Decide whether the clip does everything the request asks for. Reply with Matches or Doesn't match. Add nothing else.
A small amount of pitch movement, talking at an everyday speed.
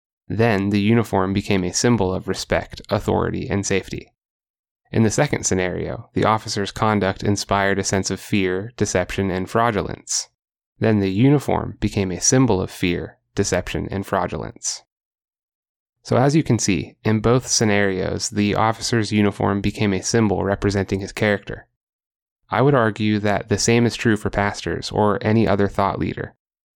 Matches